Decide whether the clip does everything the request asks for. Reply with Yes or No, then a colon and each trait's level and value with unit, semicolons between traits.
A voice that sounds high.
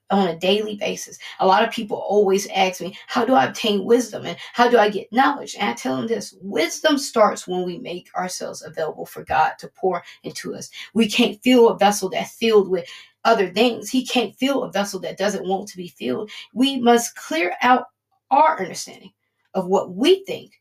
Yes: high, 215 Hz